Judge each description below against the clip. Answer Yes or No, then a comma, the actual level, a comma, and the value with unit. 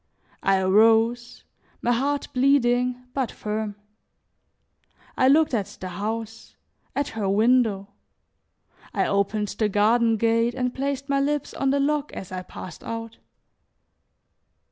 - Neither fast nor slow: No, slow, 125 wpm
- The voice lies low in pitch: No, high, 230 Hz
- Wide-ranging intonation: No, average, 4.0 semitones